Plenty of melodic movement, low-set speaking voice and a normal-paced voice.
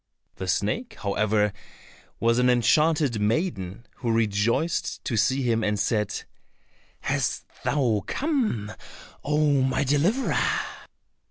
No: wide, 5.8 semitones; low, 120 Hz; slow, 105 wpm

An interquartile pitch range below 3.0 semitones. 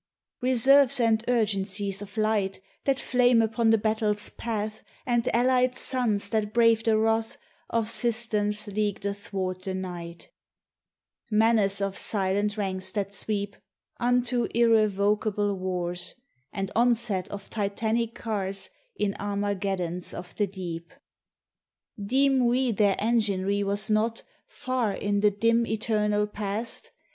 Yes: narrow, 2.5 semitones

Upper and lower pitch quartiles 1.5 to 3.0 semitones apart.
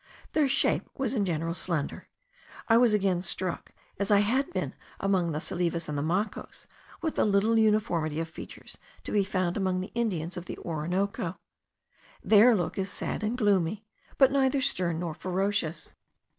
No: average, 4.2 semitones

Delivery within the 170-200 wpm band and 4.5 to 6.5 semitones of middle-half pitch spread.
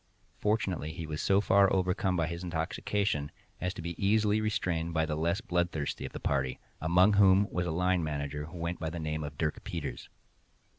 No: average, 190 wpm; average, 3.4 semitones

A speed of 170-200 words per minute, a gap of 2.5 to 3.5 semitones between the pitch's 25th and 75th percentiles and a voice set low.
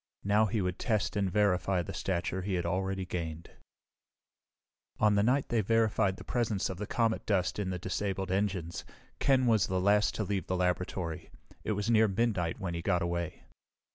Yes: average, 185 wpm; average, 2.8 semitones; very low, 95 Hz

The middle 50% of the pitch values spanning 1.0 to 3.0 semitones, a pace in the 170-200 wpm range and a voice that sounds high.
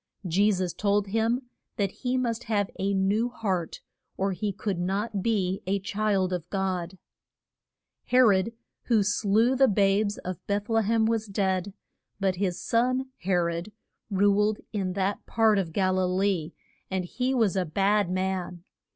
No: narrow, 2.6 semitones; average, 160 wpm; high, 200 Hz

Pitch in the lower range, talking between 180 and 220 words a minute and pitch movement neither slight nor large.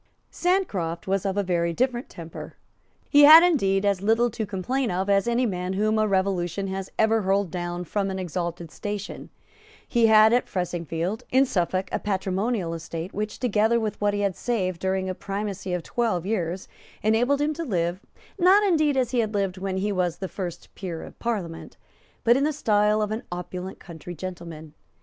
No: high, 195 Hz; average, 185 wpm; average, 3.9 semitones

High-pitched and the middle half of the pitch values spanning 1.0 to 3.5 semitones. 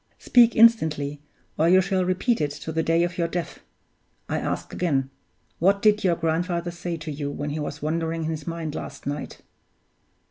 No: medium, 165 Hz; average, 3.1 semitones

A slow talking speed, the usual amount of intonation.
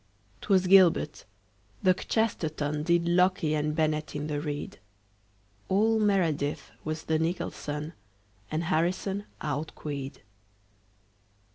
Yes: slow, 100 wpm; average, 3.6 semitones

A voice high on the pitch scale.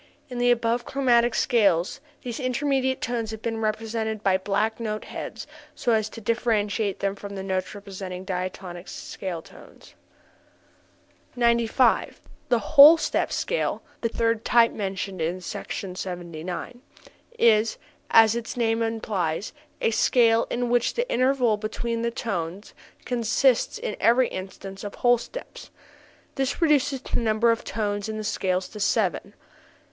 Yes: high, 225 Hz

